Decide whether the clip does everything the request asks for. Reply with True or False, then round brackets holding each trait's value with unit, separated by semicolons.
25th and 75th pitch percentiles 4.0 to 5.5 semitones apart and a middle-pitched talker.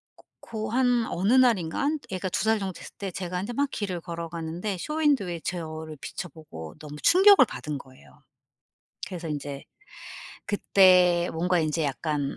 True (5.2 semitones; 180 Hz)